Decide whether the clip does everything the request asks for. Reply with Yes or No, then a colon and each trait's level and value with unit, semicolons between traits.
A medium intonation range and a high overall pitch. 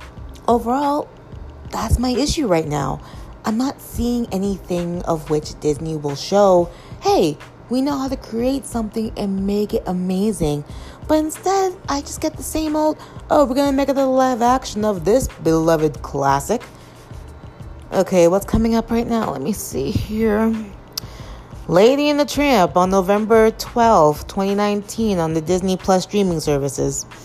No: wide, 6.4 semitones; high, 210 Hz